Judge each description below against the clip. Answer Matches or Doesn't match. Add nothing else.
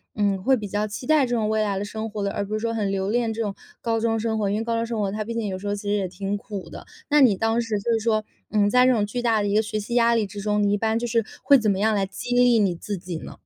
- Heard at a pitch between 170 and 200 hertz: Doesn't match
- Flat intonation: Matches